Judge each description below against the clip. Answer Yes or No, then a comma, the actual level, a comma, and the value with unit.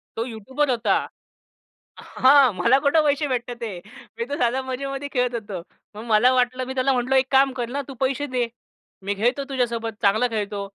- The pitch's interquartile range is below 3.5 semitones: Yes, average, 2.8 semitones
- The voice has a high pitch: Yes, very high, 250 Hz